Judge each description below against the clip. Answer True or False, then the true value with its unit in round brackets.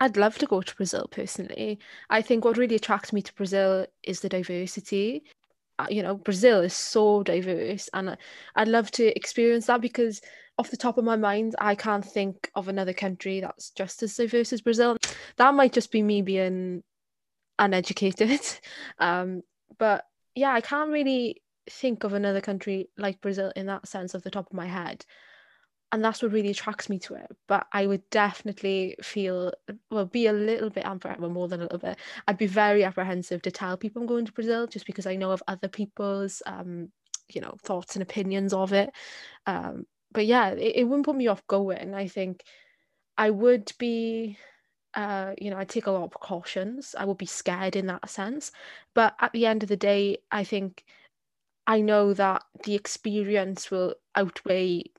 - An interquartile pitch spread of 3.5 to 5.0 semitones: False (2.8 semitones)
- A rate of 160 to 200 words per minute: True (190 wpm)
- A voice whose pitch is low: False (205 Hz)